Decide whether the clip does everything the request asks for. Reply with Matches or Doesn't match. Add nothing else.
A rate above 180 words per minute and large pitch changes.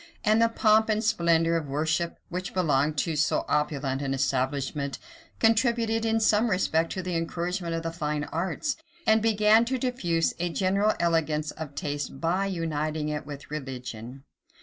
Doesn't match